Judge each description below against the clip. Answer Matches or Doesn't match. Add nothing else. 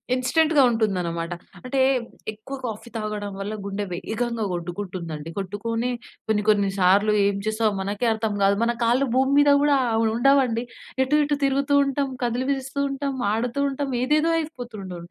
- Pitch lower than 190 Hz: Doesn't match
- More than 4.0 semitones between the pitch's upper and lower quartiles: Matches